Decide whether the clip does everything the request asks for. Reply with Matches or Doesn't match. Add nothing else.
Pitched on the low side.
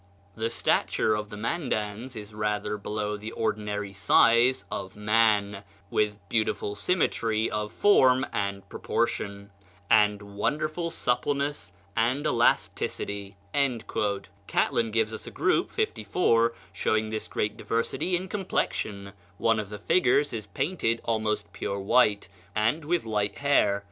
Matches